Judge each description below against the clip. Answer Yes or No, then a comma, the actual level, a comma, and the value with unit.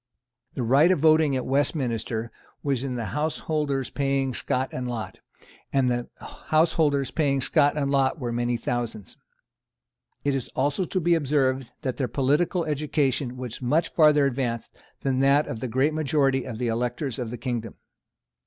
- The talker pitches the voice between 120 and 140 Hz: Yes, low, 135 Hz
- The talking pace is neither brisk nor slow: Yes, average, 165 wpm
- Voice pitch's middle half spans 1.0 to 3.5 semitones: Yes, average, 3.2 semitones